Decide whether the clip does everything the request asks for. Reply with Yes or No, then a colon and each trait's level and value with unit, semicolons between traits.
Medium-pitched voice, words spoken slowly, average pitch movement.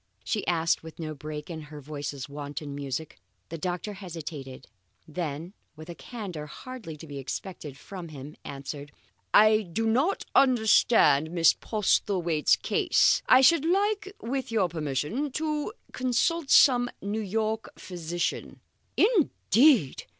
No: medium, 175 Hz; slow, 130 wpm; wide, 7.8 semitones